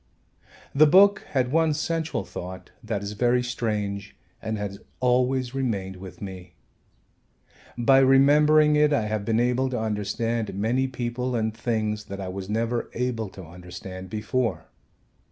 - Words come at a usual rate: Yes, average, 145 wpm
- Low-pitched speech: Yes, low, 115 Hz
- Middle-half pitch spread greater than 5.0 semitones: No, average, 4.3 semitones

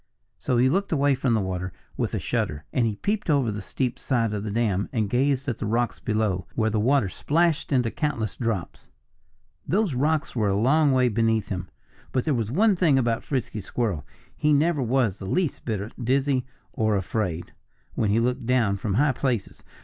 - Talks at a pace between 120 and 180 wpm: No, average, 195 wpm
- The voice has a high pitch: No, low, 120 Hz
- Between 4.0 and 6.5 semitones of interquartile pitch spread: Yes, average, 4.5 semitones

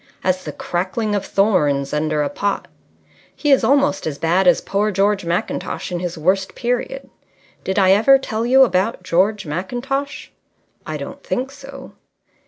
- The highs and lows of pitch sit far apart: Yes, wide, 5.8 semitones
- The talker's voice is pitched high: Yes, high, 195 Hz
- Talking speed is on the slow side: No, average, 160 wpm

